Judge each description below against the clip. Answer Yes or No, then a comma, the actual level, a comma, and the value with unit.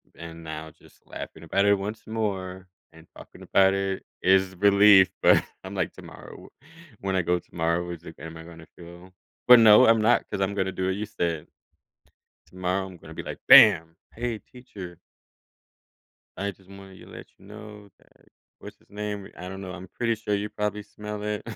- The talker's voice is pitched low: Yes, very low, 95 Hz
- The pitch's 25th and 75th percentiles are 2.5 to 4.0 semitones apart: Yes, average, 2.8 semitones